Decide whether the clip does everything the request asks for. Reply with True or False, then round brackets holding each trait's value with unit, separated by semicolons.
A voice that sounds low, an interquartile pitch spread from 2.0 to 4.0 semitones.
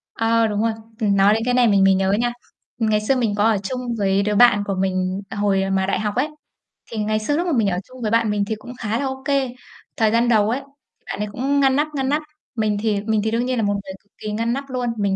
False (220 Hz; 3.4 semitones)